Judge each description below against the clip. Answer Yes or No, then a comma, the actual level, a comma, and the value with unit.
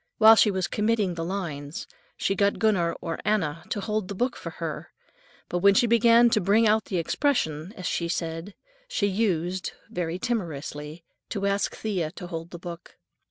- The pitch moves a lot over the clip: No, average, 4.2 semitones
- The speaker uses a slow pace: No, average, 180 wpm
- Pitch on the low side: No, high, 190 Hz